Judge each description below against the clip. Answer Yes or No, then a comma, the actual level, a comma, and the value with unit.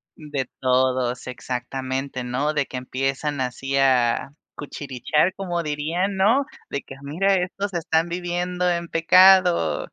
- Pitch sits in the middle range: Yes, medium, 150 Hz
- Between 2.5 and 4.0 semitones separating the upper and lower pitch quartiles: No, average, 5.3 semitones